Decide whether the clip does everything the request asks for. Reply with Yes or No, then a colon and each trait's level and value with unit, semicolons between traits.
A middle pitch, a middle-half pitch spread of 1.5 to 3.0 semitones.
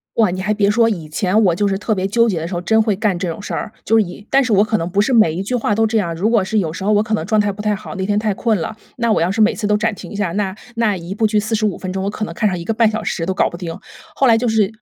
No: high, 210 Hz; average, 2.7 semitones